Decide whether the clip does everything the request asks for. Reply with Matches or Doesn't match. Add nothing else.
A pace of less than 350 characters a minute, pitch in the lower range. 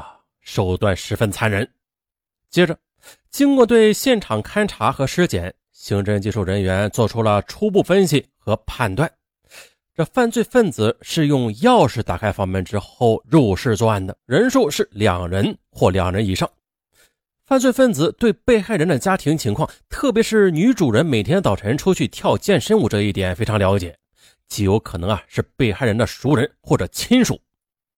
Matches